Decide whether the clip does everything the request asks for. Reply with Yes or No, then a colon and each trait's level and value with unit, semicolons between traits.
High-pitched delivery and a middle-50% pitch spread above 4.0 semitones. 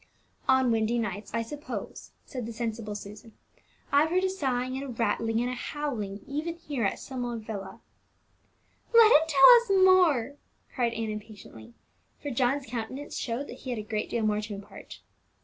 Yes: high, 240 Hz; average, 4.6 semitones